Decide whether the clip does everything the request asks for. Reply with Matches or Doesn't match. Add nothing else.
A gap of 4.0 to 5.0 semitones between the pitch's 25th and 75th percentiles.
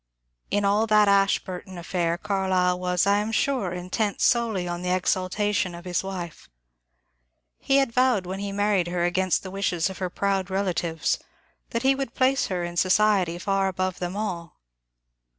Doesn't match